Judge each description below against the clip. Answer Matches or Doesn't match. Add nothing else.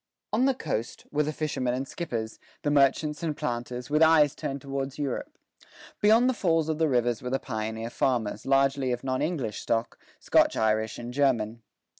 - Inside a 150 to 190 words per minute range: Matches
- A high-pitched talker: Doesn't match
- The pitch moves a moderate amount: Matches